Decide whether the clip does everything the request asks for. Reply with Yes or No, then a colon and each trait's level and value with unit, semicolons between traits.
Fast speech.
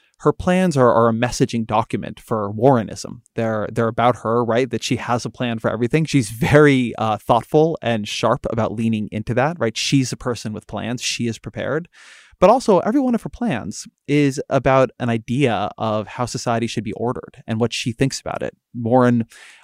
No: average, 195 wpm